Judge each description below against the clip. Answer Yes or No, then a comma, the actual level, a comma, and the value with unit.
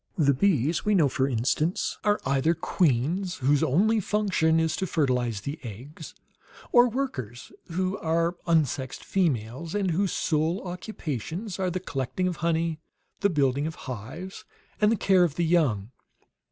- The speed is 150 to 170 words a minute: Yes, average, 155 wpm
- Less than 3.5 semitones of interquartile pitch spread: No, average, 5.3 semitones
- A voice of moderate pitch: Yes, medium, 160 Hz